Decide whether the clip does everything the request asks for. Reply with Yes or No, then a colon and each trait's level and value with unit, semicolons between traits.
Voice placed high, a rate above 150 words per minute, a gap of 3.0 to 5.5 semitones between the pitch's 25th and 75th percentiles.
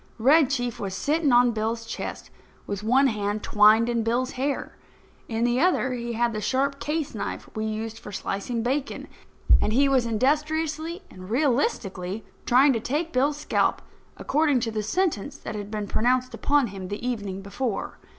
Yes: high, 240 Hz; average, 170 wpm; average, 4.5 semitones